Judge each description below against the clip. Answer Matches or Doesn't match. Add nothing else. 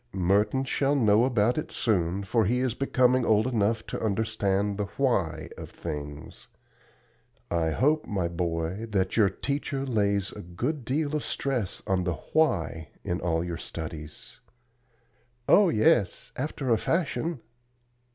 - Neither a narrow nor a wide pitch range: Doesn't match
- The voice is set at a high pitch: Doesn't match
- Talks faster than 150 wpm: Doesn't match